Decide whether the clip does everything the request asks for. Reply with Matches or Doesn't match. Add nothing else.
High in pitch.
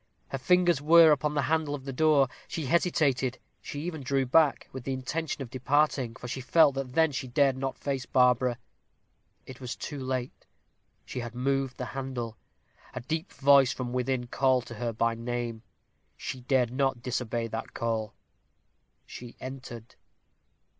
Doesn't match